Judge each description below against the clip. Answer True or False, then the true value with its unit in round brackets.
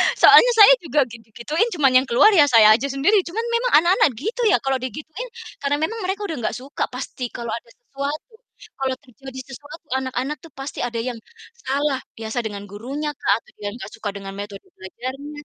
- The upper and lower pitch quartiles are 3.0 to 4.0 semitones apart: False (4.7 semitones)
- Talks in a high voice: True (270 Hz)